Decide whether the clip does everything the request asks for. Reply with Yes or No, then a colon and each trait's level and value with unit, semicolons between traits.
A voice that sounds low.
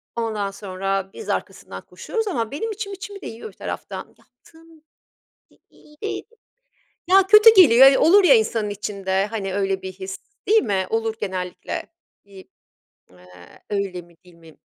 No: high, 210 Hz